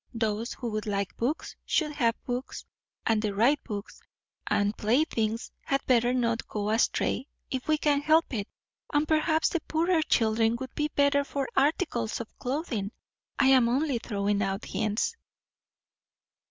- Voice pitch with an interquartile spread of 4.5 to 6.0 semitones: Yes, average, 4.9 semitones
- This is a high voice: Yes, high, 245 Hz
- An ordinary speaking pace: Yes, average, 155 wpm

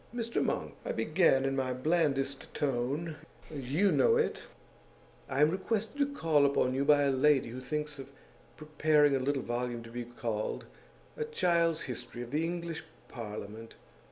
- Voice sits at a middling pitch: Yes, medium, 145 Hz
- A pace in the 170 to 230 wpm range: No, average, 160 wpm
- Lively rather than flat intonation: No, average, 4.5 semitones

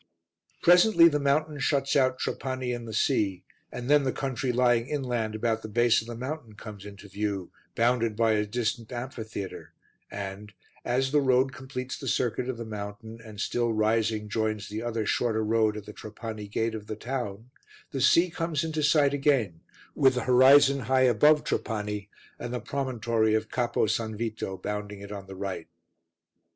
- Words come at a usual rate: Yes, average, 175 wpm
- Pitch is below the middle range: Yes, low, 115 Hz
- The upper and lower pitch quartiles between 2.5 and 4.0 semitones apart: Yes, average, 3.5 semitones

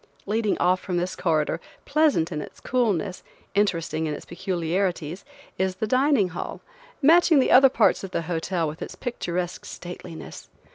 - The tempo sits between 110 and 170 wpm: Yes, average, 155 wpm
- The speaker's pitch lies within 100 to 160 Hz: No, medium, 185 Hz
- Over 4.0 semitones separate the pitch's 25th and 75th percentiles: Yes, average, 4.6 semitones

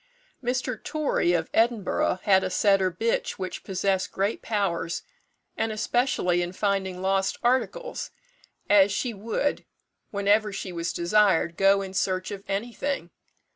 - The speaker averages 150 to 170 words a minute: No, slow, 135 wpm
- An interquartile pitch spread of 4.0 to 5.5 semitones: No, average, 3.0 semitones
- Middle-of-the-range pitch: No, high, 195 Hz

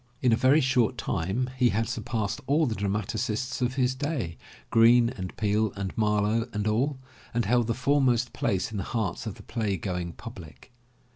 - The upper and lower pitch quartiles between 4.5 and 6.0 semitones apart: No, average, 3.5 semitones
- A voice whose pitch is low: Yes, low, 115 Hz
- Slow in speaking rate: No, average, 185 wpm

